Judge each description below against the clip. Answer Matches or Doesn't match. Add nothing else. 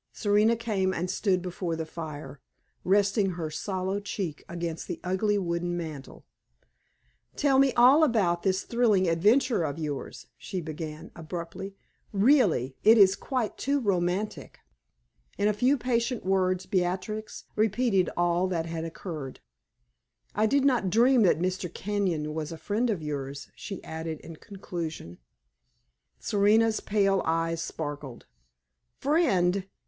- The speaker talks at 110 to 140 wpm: Matches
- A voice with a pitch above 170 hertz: Matches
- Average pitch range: Matches